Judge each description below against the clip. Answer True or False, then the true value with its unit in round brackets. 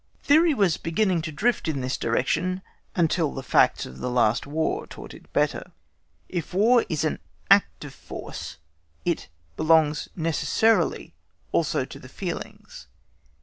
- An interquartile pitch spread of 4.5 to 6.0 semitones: True (5.1 semitones)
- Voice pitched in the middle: True (160 Hz)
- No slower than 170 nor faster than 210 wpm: False (145 wpm)